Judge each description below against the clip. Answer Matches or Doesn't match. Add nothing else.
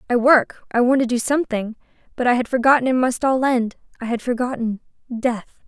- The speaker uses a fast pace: Doesn't match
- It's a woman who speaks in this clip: Matches